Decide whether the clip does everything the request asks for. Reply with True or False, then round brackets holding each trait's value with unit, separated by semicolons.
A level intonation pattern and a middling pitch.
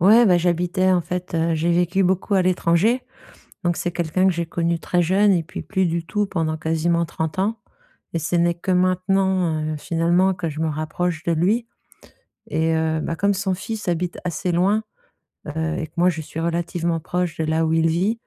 True (2.3 semitones; 175 Hz)